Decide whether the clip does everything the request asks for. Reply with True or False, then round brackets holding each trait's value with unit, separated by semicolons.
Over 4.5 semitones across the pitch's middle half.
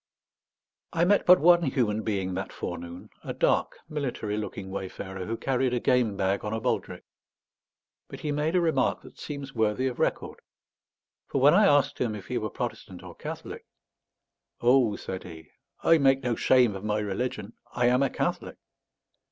True (5.3 semitones)